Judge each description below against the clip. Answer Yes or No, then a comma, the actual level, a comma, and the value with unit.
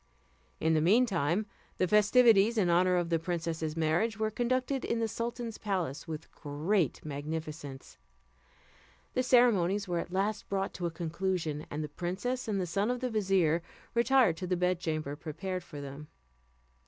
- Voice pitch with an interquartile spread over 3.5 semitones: Yes, average, 5.2 semitones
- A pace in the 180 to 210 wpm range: No, average, 165 wpm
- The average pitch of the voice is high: No, medium, 180 Hz